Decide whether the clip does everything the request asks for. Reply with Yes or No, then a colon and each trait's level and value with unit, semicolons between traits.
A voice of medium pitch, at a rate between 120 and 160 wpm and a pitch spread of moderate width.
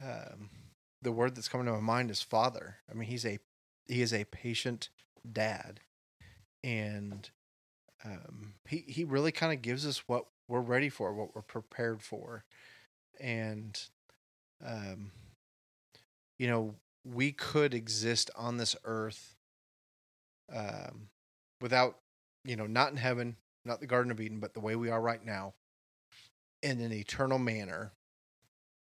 No: low, 115 Hz; average, 145 wpm; average, 3.4 semitones